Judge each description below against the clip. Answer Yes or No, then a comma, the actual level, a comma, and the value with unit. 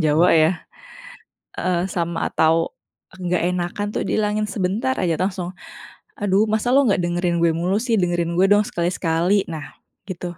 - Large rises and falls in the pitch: No, average, 3.1 semitones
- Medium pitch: Yes, medium, 180 Hz